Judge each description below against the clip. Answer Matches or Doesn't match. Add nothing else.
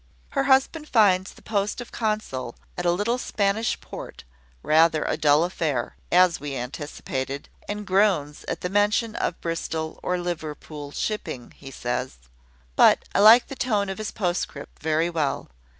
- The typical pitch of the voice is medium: Matches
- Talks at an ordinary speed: Matches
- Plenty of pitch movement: Matches